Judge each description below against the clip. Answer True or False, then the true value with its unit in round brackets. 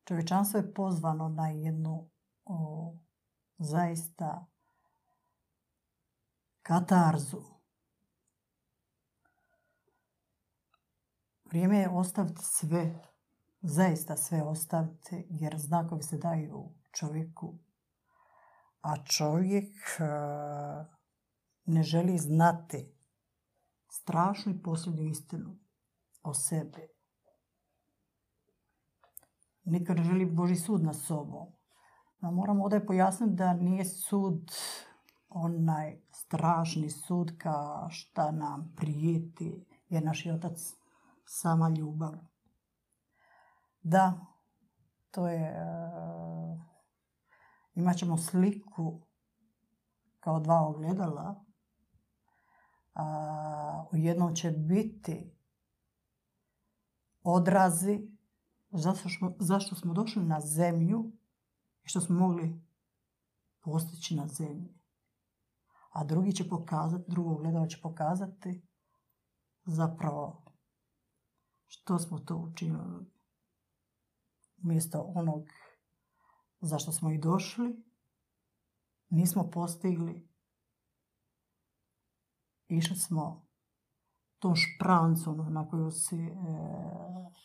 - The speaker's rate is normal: False (80 wpm)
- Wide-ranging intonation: False (2.6 semitones)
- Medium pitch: True (170 Hz)